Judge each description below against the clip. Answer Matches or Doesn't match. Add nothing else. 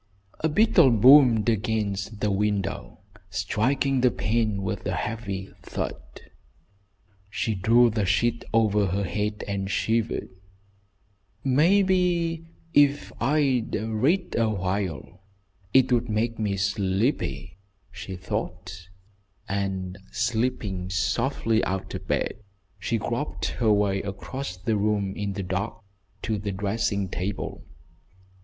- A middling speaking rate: Doesn't match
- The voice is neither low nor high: Doesn't match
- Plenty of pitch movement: Doesn't match